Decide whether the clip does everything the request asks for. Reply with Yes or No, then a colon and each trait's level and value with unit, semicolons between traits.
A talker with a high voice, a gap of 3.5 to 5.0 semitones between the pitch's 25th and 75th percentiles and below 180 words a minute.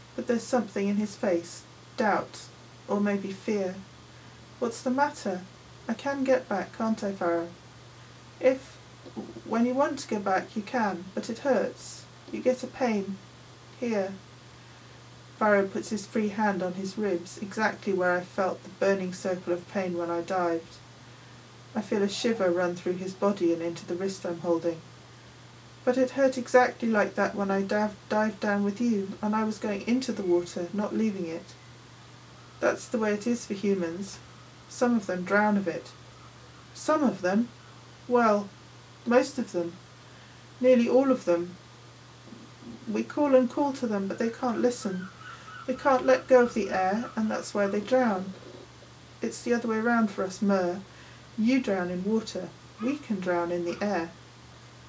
Yes: high, 205 Hz; average, 4.4 semitones; average, 170 wpm